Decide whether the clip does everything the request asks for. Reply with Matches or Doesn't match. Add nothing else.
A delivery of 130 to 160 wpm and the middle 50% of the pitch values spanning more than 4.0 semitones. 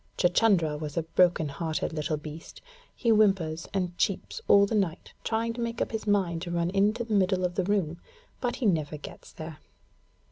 Doesn't match